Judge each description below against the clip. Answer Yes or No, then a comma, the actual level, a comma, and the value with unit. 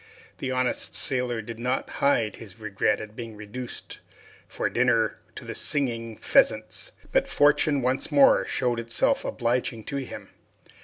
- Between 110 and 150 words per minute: Yes, average, 145 wpm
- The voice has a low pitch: Yes, low, 120 Hz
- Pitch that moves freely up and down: No, average, 2.8 semitones